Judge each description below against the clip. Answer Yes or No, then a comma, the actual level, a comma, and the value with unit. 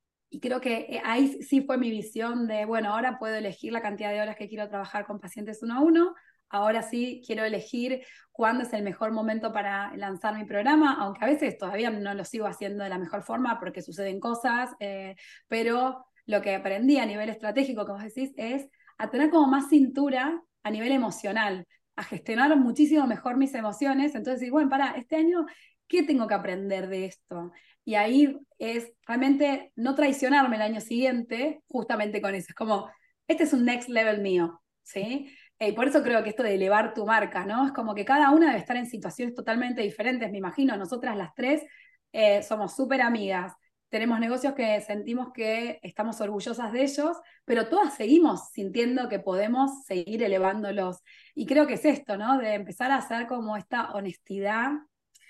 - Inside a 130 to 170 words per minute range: No, average, 185 wpm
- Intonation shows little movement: No, average, 4.7 semitones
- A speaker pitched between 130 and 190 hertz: No, high, 230 Hz